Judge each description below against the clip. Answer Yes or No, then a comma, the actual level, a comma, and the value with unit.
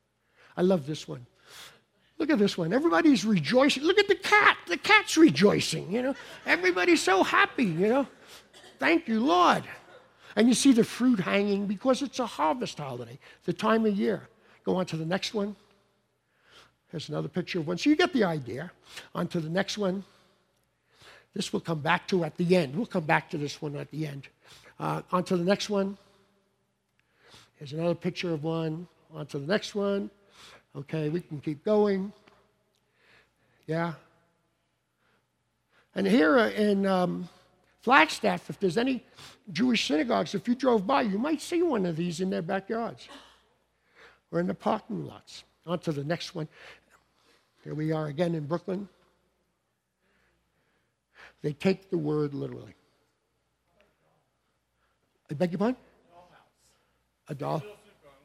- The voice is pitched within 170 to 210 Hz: Yes, medium, 185 Hz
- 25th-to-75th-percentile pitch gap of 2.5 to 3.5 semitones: No, average, 5.0 semitones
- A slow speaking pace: No, average, 155 wpm